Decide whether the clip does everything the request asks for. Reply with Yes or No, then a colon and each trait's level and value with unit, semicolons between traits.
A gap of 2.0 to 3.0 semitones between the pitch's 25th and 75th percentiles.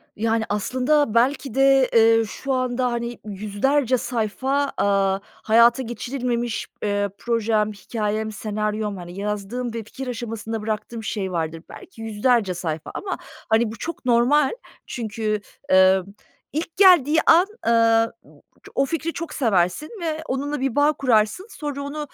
No: average, 4.2 semitones